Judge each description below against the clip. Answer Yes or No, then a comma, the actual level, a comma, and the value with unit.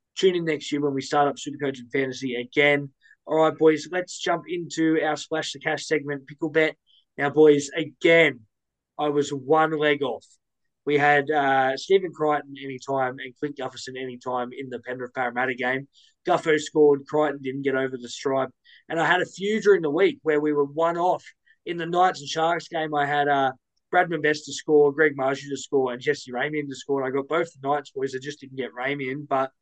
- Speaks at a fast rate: Yes, fast, 210 wpm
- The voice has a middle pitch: Yes, medium, 145 Hz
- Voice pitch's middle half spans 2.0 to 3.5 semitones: Yes, average, 2.9 semitones